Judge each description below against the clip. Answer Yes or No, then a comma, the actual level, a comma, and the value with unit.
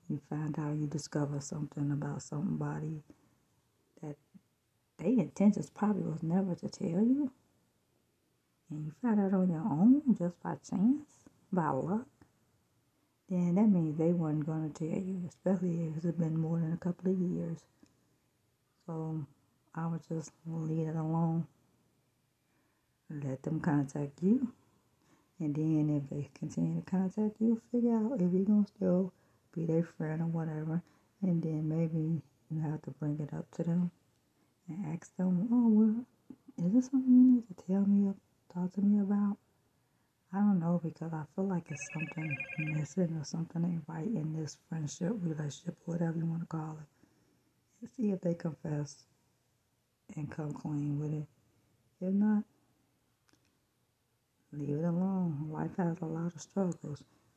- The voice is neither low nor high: Yes, medium, 165 Hz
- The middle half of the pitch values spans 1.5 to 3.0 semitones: No, average, 3.9 semitones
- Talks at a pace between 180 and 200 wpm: No, average, 160 wpm